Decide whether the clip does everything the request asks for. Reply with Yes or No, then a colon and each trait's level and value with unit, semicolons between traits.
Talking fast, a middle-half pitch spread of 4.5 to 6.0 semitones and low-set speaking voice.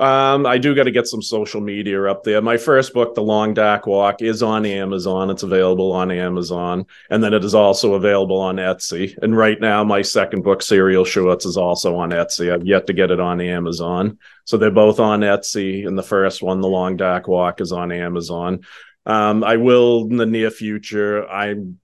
No: fast, 210 wpm; average, 2.8 semitones; low, 100 Hz